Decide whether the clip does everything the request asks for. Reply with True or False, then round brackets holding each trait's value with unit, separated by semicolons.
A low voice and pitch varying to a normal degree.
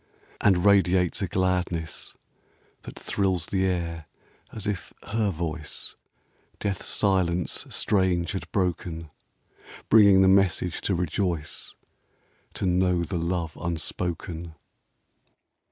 False (90 Hz; 2.1 semitones)